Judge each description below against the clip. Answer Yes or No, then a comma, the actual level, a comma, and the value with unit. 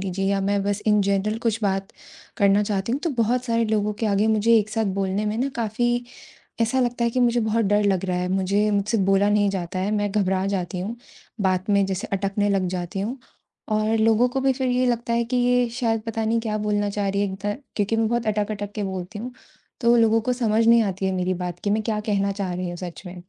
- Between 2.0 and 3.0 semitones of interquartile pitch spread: Yes, average, 2.7 semitones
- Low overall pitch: No, high, 210 Hz